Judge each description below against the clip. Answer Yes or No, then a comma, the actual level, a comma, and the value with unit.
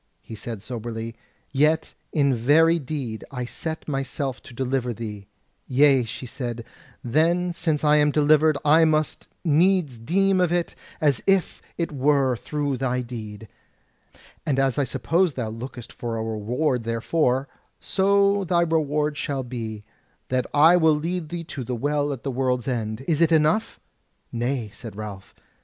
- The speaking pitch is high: No, medium, 140 Hz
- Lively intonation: No, average, 4.8 semitones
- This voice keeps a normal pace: Yes, average, 155 wpm